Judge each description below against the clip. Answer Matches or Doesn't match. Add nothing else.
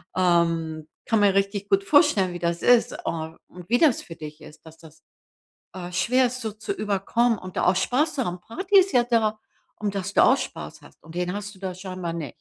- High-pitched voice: Matches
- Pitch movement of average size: Matches